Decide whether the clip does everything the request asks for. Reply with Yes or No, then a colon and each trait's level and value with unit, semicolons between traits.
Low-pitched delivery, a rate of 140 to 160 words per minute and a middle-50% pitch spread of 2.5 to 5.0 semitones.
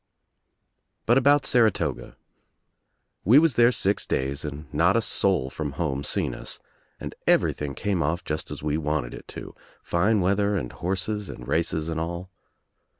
No: very low, 85 Hz; average, 155 wpm; wide, 5.6 semitones